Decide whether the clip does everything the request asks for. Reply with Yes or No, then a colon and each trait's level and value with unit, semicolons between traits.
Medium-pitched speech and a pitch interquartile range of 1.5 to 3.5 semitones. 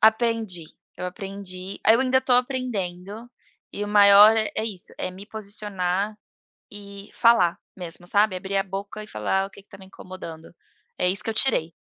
No: high, 200 Hz; average, 2.9 semitones